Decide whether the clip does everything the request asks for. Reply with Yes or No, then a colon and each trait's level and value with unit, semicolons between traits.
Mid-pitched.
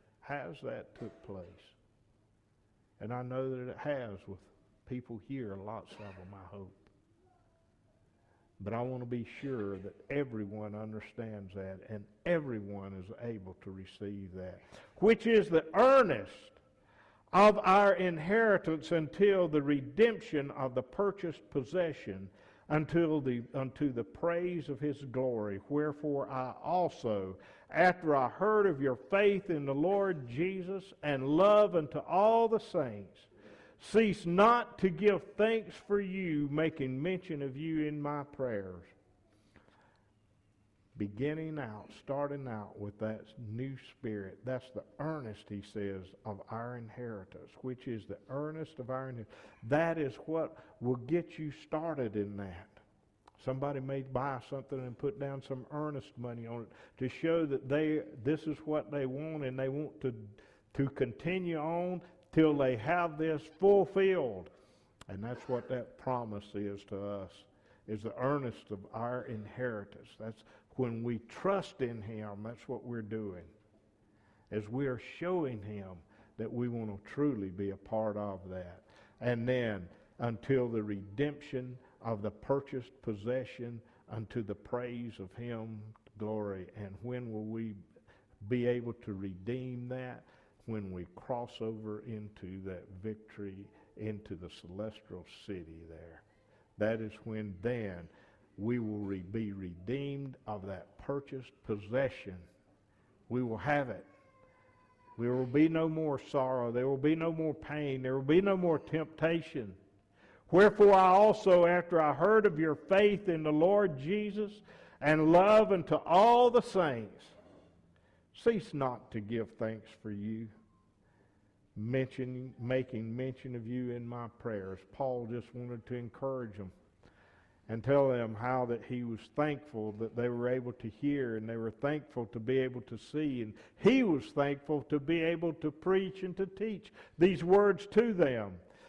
No: low, 125 Hz